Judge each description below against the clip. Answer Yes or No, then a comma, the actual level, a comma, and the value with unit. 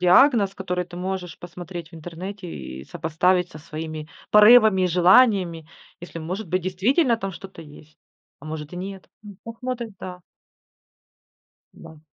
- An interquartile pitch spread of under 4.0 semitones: Yes, average, 3.3 semitones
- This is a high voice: No, medium, 180 Hz